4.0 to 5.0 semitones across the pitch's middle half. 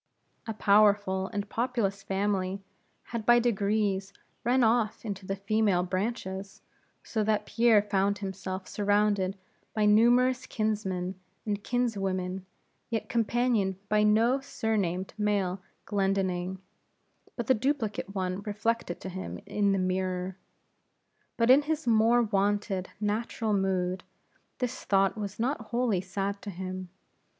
No: average, 2.8 semitones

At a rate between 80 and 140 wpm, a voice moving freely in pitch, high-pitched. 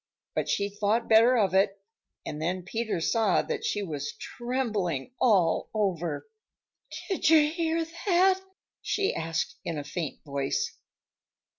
Yes: slow, 135 wpm; wide, 7.5 semitones; high, 205 Hz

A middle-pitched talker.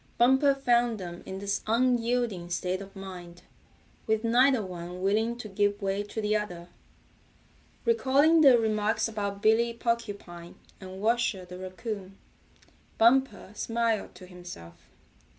No: high, 210 Hz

